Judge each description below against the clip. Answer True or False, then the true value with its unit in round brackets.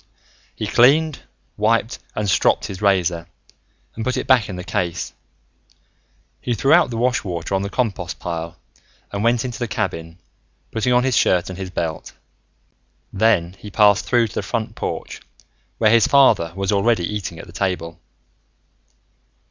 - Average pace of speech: True (165 wpm)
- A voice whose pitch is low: True (105 Hz)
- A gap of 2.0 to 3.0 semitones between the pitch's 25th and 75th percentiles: False (4.8 semitones)